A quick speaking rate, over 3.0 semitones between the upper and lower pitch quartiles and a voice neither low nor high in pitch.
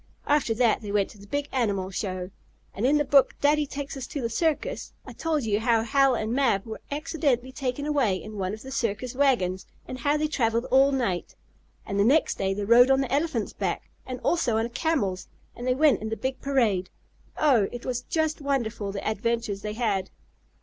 No: fast, 210 wpm; average, 4.8 semitones; high, 245 Hz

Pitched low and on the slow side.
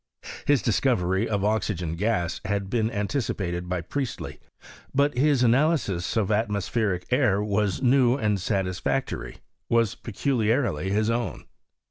Yes: low, 110 Hz; slow, 130 wpm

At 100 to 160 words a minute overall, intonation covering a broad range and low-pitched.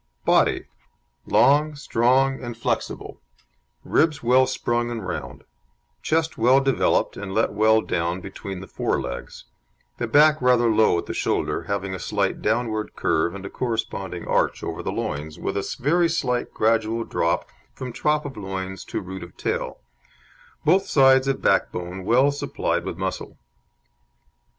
Yes: average, 150 wpm; wide, 5.7 semitones; low, 115 Hz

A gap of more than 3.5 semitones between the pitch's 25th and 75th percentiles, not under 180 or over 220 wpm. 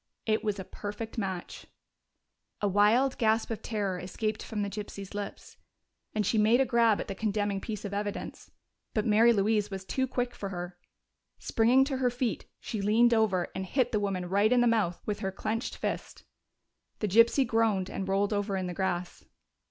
No: narrow, 2.6 semitones; average, 190 wpm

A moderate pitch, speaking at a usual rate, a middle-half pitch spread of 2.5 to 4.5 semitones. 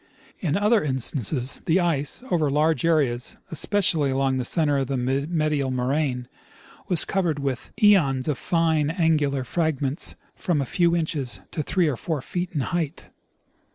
Yes: medium, 150 Hz; average, 155 wpm; average, 3.8 semitones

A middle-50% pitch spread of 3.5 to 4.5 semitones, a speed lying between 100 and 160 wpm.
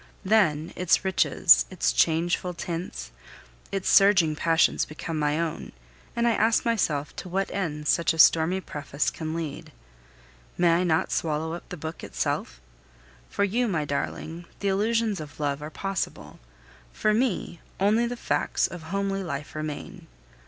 Yes: average, 4.2 semitones; average, 150 wpm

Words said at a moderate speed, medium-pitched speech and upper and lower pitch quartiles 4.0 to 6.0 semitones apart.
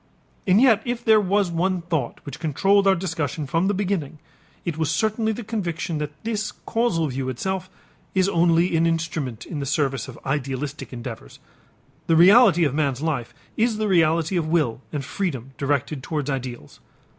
Yes: average, 170 wpm; medium, 165 Hz; average, 5.3 semitones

